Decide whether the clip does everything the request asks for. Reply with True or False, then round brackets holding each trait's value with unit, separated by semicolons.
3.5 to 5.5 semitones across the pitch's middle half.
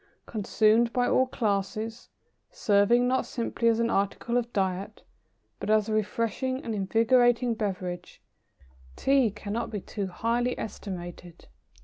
False (3.0 semitones)